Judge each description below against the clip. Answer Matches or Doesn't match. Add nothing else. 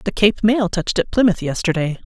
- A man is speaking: Doesn't match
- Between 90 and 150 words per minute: Doesn't match